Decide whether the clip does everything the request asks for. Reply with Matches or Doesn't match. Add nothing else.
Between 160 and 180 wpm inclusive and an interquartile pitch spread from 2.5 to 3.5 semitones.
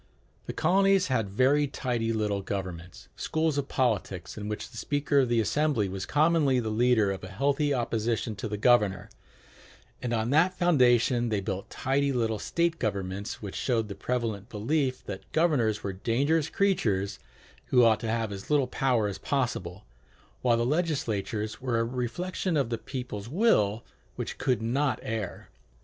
Doesn't match